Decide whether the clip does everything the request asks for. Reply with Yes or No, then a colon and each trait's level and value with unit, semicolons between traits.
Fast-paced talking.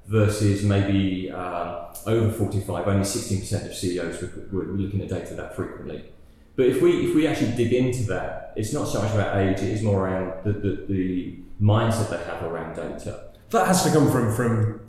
No: average, 195 wpm